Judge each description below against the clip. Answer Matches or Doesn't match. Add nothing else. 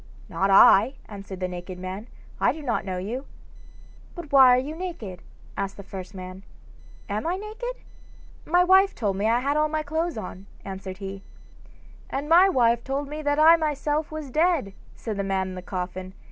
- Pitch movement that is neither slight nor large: Doesn't match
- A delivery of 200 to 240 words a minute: Doesn't match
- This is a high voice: Matches